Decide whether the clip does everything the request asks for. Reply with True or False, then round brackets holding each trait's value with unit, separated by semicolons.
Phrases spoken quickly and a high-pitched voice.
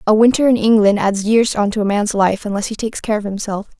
True (270 wpm; 210 Hz)